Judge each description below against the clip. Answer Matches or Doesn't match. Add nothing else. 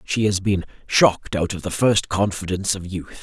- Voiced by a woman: Doesn't match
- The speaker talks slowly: Doesn't match